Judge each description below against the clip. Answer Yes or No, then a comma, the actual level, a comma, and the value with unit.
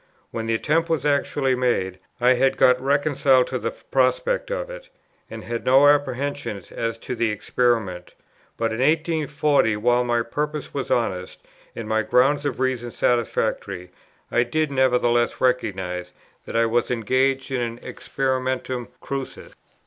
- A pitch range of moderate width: Yes, average, 3.4 semitones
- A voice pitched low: Yes, low, 125 Hz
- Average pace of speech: Yes, average, 150 wpm